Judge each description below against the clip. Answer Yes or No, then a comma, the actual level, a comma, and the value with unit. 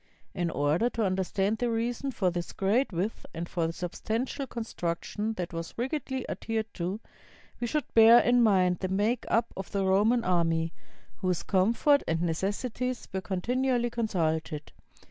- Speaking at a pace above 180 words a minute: No, average, 160 wpm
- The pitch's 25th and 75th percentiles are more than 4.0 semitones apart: Yes, average, 5.0 semitones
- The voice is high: Yes, high, 200 Hz